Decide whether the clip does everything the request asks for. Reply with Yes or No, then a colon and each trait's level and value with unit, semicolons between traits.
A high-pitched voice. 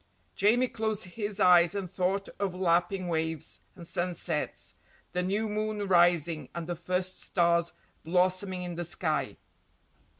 No: medium, 180 Hz